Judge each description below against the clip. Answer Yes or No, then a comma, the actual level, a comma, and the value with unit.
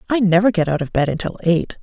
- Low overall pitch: No, medium, 185 Hz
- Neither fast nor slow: No, fast, 265 wpm